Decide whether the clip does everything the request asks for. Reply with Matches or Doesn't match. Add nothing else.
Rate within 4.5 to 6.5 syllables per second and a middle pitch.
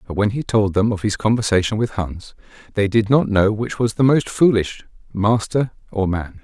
Doesn't match